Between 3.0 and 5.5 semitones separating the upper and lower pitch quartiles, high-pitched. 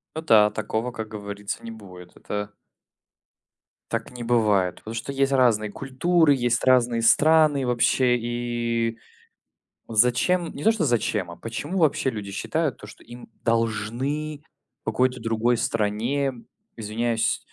No: average, 3.6 semitones; low, 120 Hz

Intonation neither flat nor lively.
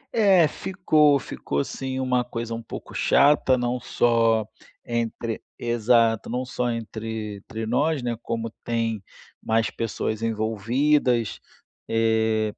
No: narrow, 2.2 semitones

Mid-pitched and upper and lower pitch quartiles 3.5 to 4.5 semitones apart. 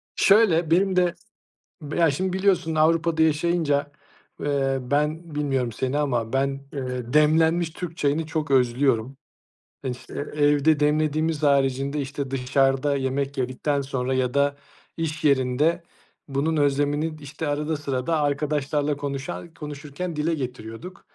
No: medium, 145 Hz; average, 2.8 semitones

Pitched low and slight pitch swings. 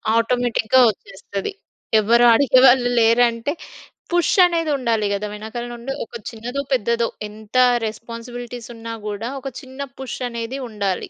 No: high, 235 Hz; narrow, 2.2 semitones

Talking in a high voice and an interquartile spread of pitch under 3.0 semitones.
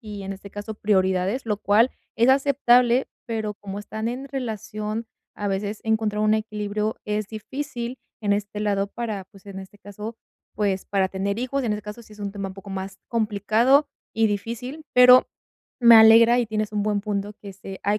Yes: high, 210 Hz; narrow, 2.4 semitones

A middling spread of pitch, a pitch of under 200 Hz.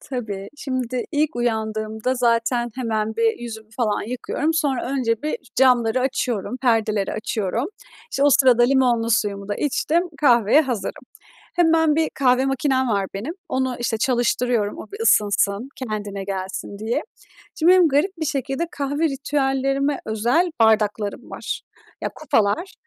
No: average, 4.0 semitones; high, 245 Hz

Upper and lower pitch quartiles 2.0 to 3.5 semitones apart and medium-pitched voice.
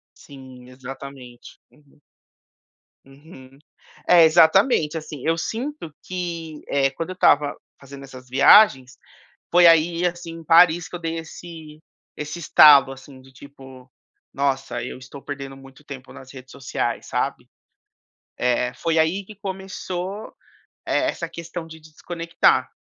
No: average, 3.9 semitones; medium, 150 Hz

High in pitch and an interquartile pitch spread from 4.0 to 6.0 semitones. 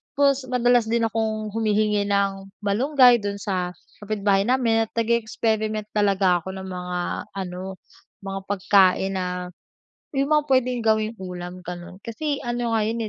No: high, 215 Hz; average, 3.3 semitones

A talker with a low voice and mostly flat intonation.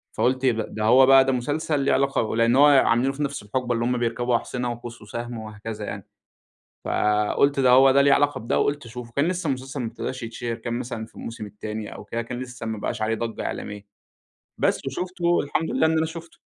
No: low, 125 Hz; average, 3.4 semitones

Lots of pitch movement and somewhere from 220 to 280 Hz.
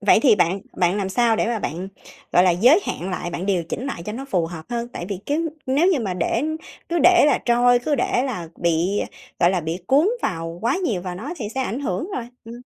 No: wide, 6.3 semitones; high, 210 Hz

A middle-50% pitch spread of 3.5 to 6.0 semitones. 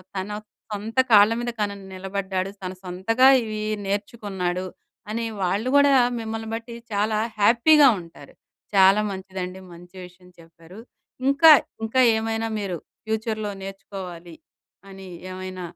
No: average, 3.1 semitones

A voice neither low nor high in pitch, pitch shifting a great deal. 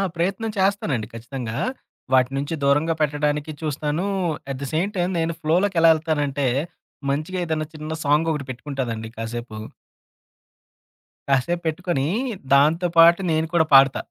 No: medium, 150 Hz; average, 3.4 semitones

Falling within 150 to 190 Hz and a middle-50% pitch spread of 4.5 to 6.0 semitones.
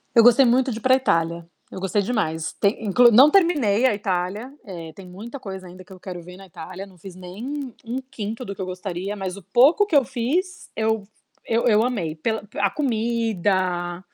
No: high, 205 Hz; average, 5.0 semitones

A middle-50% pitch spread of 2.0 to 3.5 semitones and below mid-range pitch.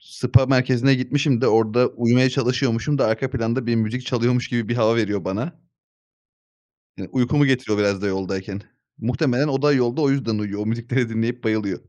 Yes: average, 3.0 semitones; low, 120 Hz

